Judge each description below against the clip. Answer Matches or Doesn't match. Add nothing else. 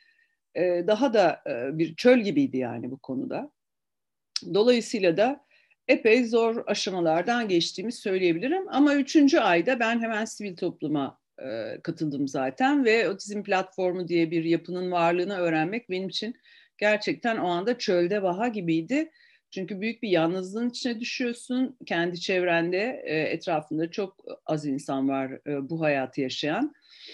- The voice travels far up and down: Matches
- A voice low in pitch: Doesn't match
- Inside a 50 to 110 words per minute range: Doesn't match